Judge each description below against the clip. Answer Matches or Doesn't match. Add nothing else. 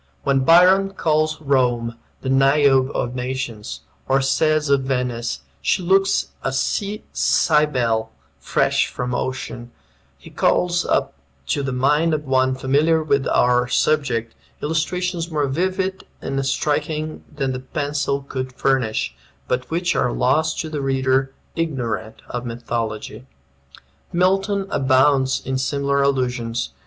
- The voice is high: Doesn't match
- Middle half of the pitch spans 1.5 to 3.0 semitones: Doesn't match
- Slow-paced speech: Matches